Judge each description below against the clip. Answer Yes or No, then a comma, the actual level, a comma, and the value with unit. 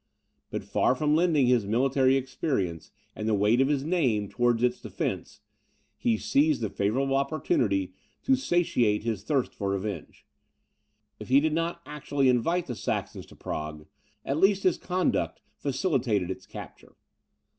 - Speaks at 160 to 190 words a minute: No, average, 150 wpm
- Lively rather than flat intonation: Yes, wide, 6.0 semitones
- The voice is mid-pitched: No, low, 130 Hz